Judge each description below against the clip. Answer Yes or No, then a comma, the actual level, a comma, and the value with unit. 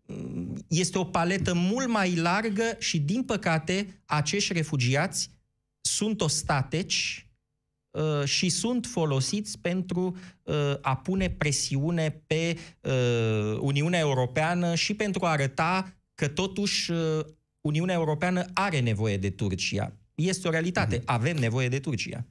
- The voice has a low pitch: No, medium, 160 Hz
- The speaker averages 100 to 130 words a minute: Yes, average, 120 wpm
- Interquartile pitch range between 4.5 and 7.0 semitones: Yes, average, 5.1 semitones